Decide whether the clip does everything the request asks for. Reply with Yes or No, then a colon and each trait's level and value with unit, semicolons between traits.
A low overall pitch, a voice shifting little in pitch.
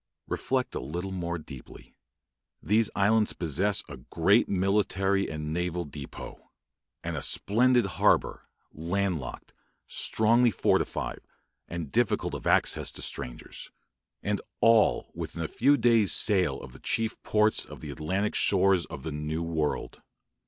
No: very low, 95 Hz; average, 4.9 semitones